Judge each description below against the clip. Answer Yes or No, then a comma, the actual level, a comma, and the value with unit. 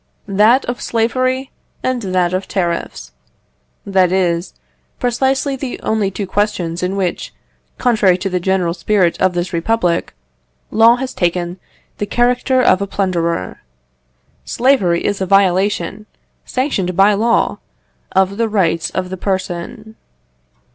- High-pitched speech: Yes, high, 195 Hz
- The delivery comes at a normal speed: No, slow, 130 wpm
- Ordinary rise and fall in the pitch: Yes, average, 4.3 semitones